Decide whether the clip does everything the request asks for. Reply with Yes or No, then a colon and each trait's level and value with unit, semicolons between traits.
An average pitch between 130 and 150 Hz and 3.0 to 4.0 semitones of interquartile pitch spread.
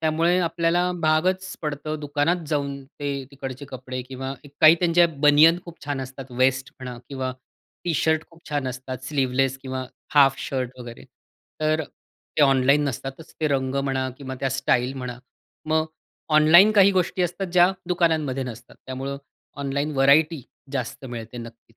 Yes: medium, 140 Hz; average, 3.3 semitones